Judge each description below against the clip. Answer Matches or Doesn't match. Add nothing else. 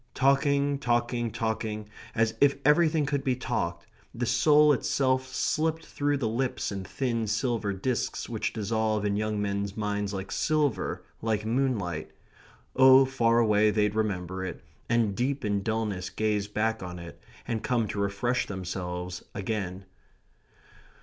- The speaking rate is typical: Matches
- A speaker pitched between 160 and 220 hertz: Doesn't match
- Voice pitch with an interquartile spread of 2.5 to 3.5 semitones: Doesn't match